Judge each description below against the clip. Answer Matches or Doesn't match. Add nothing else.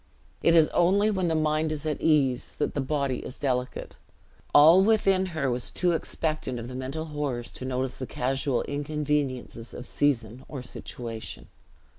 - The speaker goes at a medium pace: Matches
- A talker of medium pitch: Matches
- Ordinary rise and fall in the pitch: Matches